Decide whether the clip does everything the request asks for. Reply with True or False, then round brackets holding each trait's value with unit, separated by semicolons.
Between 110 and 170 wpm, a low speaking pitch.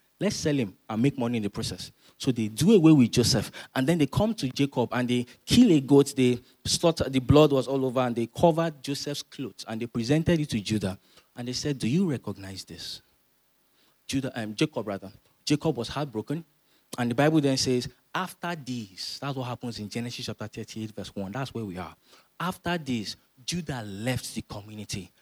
False (200 wpm; 125 Hz)